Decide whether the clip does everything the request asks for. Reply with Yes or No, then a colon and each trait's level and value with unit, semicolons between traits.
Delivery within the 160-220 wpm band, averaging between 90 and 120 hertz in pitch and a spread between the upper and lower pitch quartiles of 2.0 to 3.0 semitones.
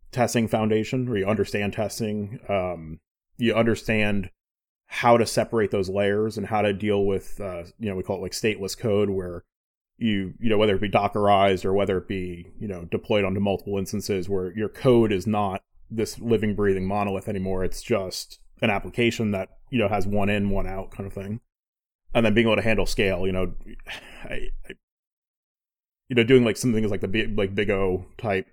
Yes: average, 200 wpm; low, 100 Hz; narrow, 2.4 semitones